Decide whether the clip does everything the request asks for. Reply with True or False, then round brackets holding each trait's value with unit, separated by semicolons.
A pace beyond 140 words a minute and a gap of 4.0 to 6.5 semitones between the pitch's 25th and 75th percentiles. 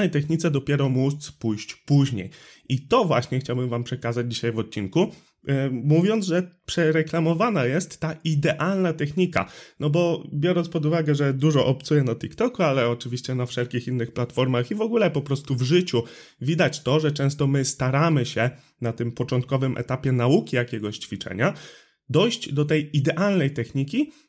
True (160 wpm; 4.8 semitones)